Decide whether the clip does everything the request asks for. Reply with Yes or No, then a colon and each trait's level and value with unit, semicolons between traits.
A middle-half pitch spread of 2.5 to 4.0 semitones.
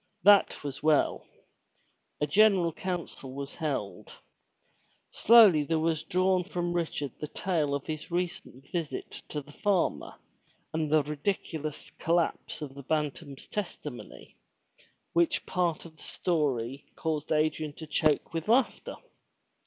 Yes: average, 3.1 semitones